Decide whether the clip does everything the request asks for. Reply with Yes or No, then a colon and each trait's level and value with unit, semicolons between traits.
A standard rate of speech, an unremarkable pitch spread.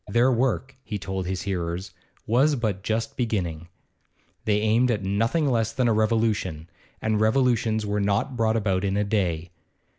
Yes: average, 160 wpm; average, 3.1 semitones